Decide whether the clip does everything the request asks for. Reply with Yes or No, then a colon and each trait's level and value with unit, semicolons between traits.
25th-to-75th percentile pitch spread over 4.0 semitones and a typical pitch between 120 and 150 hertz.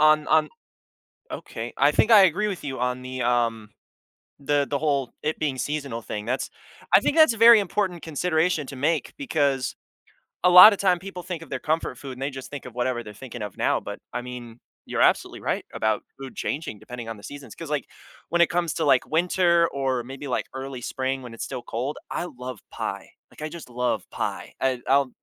Yes: average, 4.8 semitones; medium, 140 Hz